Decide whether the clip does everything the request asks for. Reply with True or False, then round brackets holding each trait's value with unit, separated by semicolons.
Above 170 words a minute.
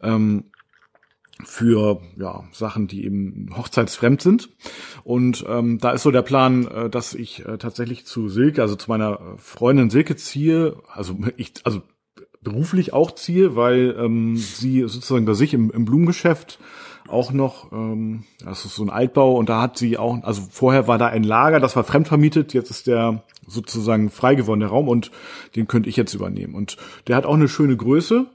True (185 wpm)